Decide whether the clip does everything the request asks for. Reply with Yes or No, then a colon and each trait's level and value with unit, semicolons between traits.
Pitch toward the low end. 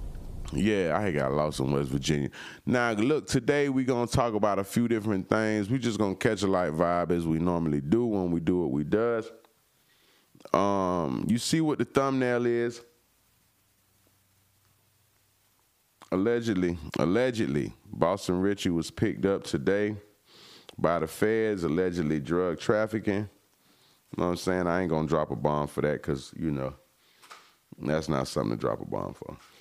Yes: very low, 95 Hz